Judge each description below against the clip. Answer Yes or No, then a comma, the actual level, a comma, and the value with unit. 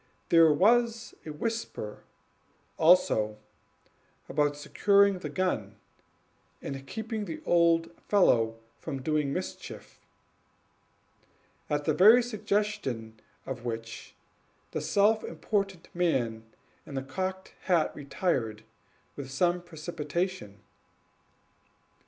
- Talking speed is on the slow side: Yes, slow, 95 wpm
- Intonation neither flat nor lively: No, wide, 6.4 semitones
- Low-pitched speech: No, medium, 165 Hz